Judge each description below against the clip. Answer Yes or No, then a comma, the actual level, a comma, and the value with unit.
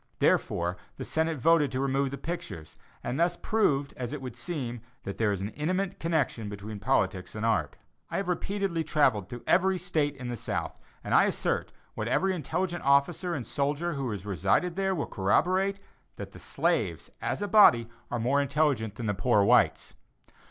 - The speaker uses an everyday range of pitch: No, wide, 7.2 semitones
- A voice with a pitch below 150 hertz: Yes, medium, 140 Hz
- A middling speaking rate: Yes, average, 185 wpm